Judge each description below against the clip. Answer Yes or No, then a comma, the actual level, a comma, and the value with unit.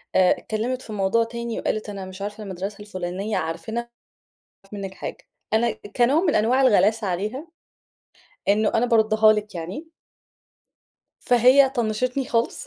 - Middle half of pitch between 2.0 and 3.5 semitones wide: Yes, average, 3.2 semitones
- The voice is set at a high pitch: Yes, high, 215 Hz